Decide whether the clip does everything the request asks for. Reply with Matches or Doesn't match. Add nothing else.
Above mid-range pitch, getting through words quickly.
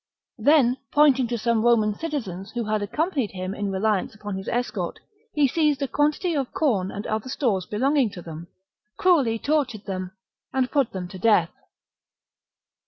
Doesn't match